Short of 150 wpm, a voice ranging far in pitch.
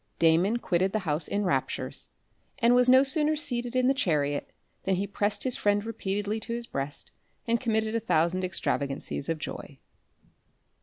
No: average, 165 wpm; wide, 5.7 semitones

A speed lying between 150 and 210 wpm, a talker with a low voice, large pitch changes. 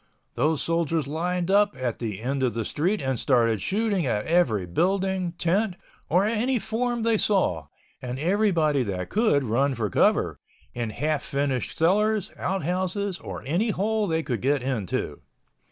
No: average, 155 wpm; medium, 165 Hz; wide, 7.5 semitones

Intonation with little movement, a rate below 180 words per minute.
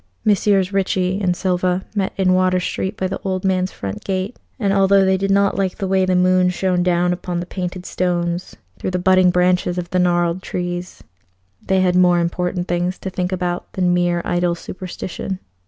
No: narrow, 1.1 semitones; average, 190 wpm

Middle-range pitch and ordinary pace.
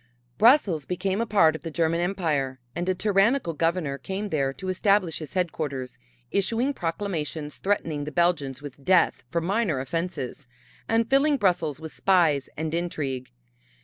Yes: medium, 170 Hz; average, 150 wpm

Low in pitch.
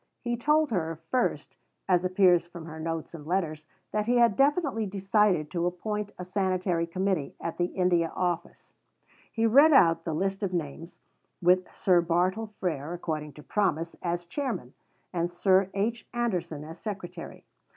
No: medium, 180 Hz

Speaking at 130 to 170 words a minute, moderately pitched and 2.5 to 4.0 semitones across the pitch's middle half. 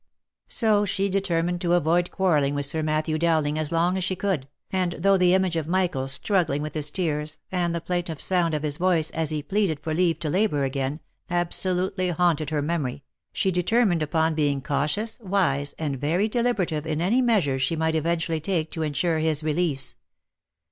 No: average, 185 wpm; medium, 165 Hz; average, 3.2 semitones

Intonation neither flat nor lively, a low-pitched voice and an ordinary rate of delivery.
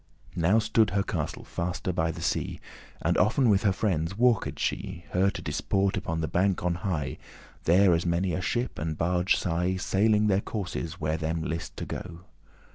Yes: average, 3.2 semitones; very low, 90 Hz; average, 190 wpm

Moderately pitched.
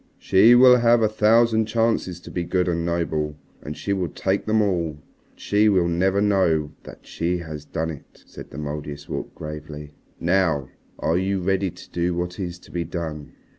No: very low, 90 Hz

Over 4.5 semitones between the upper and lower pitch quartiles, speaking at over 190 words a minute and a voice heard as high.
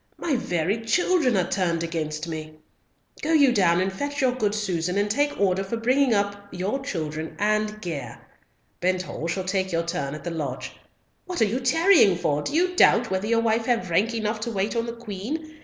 Yes: wide, 5.4 semitones; average, 200 wpm; high, 205 Hz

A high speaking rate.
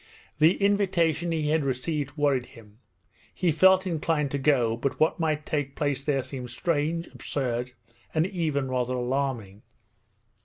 No: average, 145 wpm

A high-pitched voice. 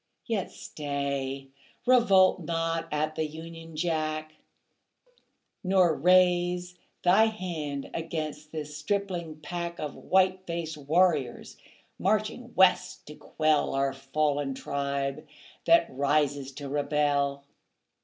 No: medium, 155 Hz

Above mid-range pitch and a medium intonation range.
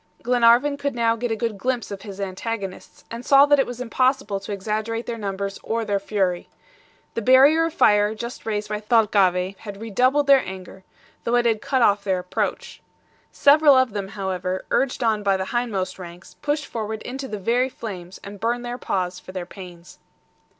Yes: high, 220 Hz; average, 4.0 semitones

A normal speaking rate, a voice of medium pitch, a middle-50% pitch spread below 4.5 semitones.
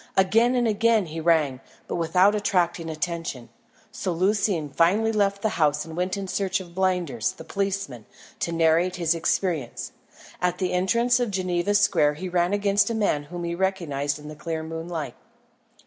Yes: average, 170 wpm; medium, 180 Hz; average, 3.5 semitones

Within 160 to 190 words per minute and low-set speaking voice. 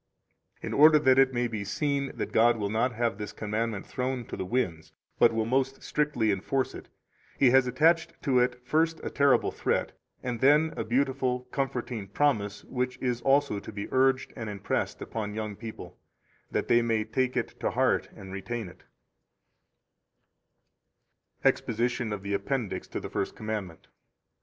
Yes: average, 170 wpm; low, 120 Hz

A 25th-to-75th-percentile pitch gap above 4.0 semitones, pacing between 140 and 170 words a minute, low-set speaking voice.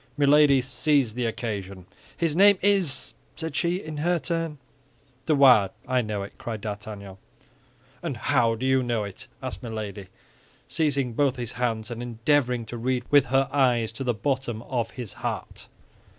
Yes: average, 4.4 semitones; average, 165 wpm; low, 125 Hz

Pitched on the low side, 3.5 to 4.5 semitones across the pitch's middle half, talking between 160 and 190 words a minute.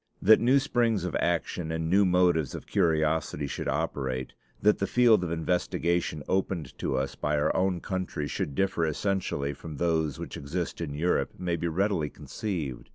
Yes: very low, 85 Hz; average, 3.8 semitones; average, 170 wpm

